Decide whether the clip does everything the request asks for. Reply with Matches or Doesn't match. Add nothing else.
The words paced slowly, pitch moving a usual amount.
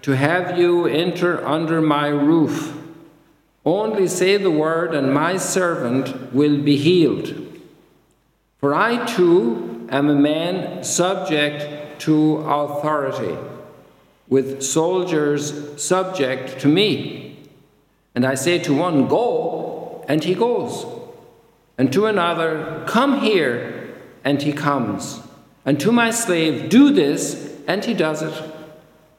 Matches